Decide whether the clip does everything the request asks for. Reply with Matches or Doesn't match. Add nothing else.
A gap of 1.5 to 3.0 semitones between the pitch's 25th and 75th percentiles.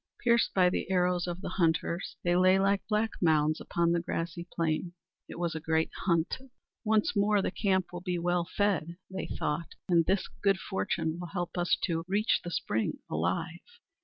Matches